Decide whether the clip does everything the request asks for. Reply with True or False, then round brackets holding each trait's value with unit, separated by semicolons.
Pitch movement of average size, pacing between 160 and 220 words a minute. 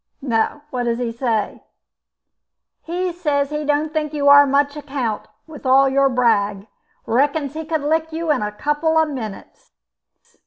True (3.7 semitones; 165 wpm)